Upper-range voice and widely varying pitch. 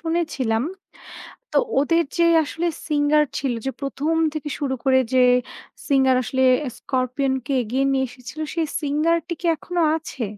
No: very high, 280 Hz; average, 3.5 semitones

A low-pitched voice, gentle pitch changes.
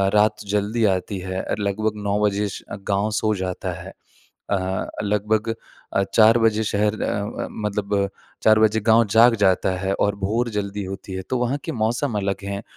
Yes: low, 105 Hz; narrow, 1.8 semitones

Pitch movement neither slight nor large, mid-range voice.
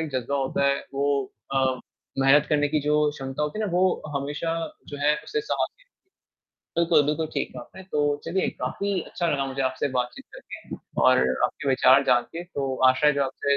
Yes: average, 3.0 semitones; medium, 145 Hz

